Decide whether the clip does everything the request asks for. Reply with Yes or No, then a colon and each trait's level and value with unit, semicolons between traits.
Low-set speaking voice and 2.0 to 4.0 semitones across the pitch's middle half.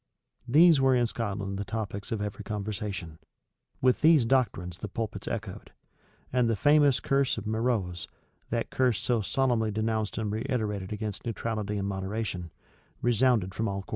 Yes: low, 110 Hz; average, 3.4 semitones